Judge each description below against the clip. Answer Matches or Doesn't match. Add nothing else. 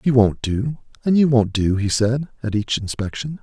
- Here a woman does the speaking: Doesn't match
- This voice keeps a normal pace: Doesn't match